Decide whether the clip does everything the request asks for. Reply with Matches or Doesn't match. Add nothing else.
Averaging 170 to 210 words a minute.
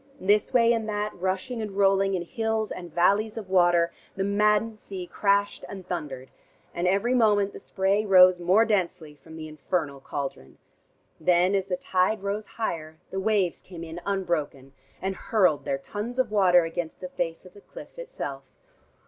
Matches